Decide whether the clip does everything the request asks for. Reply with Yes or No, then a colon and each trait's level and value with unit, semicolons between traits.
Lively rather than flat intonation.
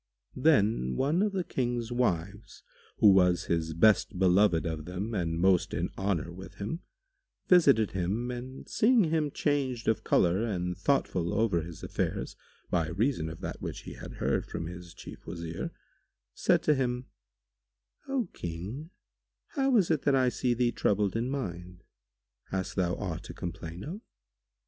Yes: wide, 6.8 semitones